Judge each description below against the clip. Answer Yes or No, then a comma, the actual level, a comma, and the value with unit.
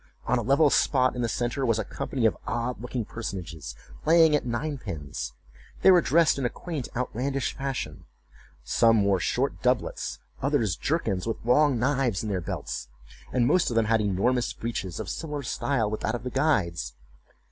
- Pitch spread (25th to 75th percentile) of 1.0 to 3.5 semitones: No, average, 4.4 semitones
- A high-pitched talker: No, low, 120 Hz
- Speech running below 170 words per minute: No, average, 180 wpm